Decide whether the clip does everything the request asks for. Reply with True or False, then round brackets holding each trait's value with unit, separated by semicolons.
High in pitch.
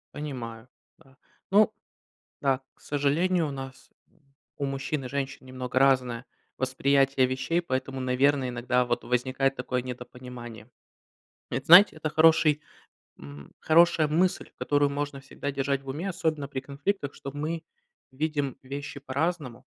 False (135 Hz)